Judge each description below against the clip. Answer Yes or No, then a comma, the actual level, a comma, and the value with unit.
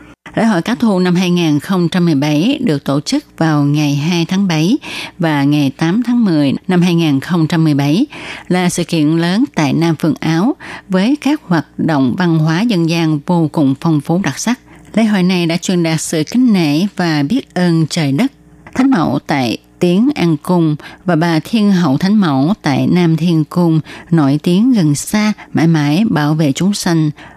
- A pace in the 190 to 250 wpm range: No, average, 180 wpm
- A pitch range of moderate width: Yes, average, 4.3 semitones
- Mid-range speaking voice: Yes, medium, 170 Hz